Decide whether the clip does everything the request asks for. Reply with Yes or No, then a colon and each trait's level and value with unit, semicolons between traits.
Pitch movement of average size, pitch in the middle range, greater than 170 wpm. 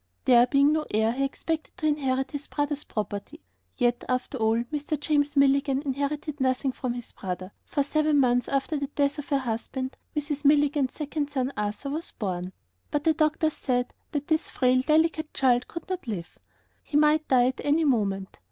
No: average, 3.2 semitones; very high, 275 Hz; average, 180 wpm